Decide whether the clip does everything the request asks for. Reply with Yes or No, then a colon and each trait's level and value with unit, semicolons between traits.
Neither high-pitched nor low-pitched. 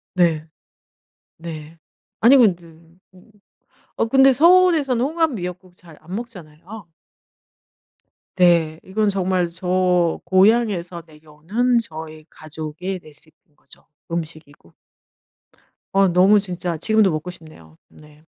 Yes: medium, 180 Hz